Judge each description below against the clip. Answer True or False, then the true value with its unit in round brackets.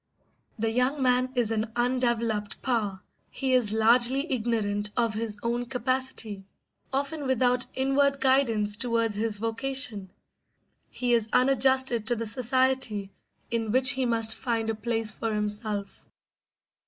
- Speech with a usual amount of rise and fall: True (3.0 semitones)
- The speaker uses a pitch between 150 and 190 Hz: False (235 Hz)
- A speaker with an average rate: False (130 wpm)